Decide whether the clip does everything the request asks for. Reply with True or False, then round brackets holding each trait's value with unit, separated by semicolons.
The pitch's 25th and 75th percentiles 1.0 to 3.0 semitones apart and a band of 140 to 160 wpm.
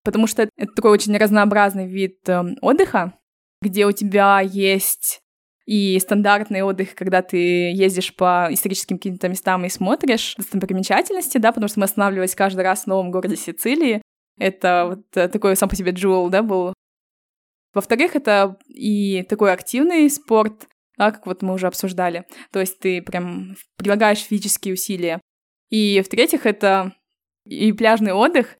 True (2.4 semitones; 150 wpm)